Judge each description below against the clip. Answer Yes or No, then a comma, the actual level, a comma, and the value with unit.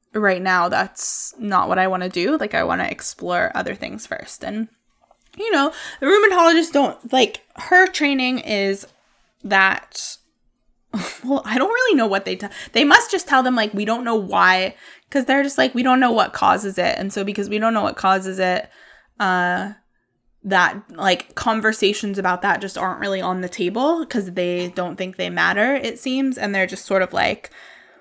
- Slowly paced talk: No, average, 195 wpm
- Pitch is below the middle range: No, high, 215 Hz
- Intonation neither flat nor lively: No, wide, 6.0 semitones